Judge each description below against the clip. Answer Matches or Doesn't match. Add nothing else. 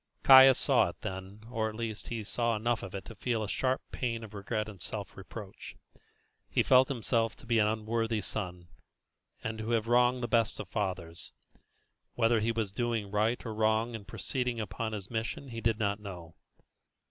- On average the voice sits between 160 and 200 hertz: Doesn't match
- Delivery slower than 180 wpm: Doesn't match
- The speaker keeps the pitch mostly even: Matches